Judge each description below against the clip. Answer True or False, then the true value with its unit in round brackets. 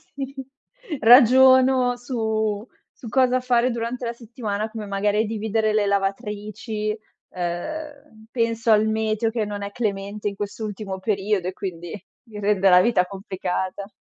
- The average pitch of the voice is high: True (215 Hz)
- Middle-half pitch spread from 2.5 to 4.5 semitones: True (2.8 semitones)